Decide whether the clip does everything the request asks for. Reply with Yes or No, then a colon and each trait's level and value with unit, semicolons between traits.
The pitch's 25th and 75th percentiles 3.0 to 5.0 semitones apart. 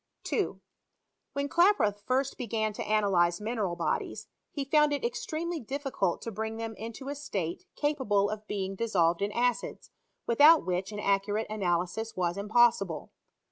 No: wide, 5.5 semitones